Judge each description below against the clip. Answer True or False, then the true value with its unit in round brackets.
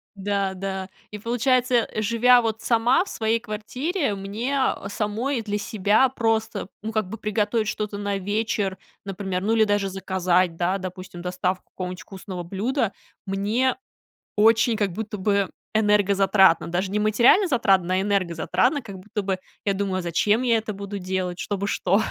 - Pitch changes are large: False (2.8 semitones)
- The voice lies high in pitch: True (205 Hz)